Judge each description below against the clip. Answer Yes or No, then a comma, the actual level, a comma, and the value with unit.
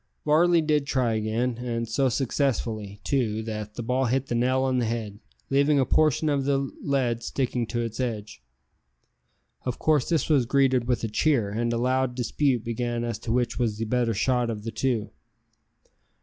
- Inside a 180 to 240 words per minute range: Yes, average, 185 wpm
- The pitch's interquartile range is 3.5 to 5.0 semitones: No, average, 2.8 semitones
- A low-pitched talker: Yes, low, 120 Hz